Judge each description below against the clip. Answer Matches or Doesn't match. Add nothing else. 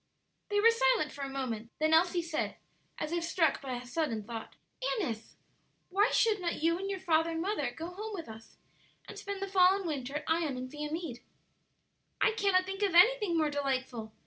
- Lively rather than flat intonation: Matches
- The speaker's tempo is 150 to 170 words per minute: Doesn't match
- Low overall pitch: Doesn't match